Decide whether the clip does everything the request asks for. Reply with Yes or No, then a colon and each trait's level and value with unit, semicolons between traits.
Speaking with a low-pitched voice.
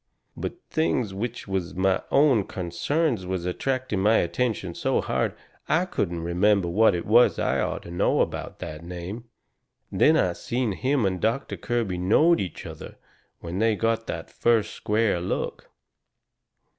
Yes: low, 105 Hz